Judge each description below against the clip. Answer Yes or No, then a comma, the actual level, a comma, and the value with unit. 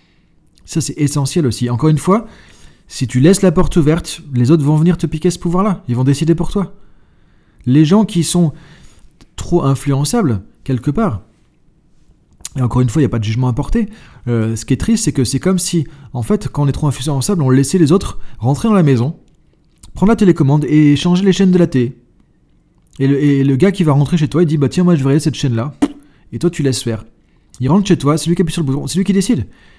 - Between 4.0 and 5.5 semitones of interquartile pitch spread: Yes, average, 4.8 semitones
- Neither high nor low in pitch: Yes, medium, 150 Hz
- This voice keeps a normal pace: No, fast, 240 wpm